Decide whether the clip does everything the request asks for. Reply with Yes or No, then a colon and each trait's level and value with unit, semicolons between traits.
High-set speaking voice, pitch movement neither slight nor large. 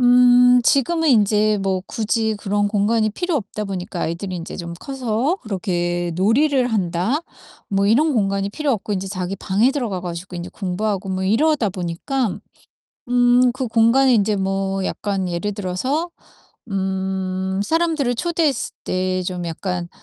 Yes: high, 205 Hz; average, 4.8 semitones